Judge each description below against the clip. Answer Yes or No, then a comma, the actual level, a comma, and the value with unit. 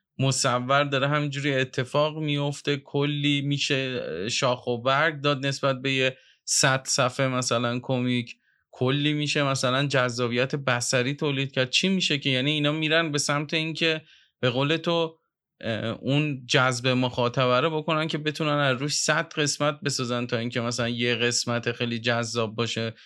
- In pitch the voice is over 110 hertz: Yes, low, 135 Hz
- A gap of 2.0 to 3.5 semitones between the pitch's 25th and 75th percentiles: Yes, average, 2.9 semitones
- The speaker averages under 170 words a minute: Yes, average, 150 wpm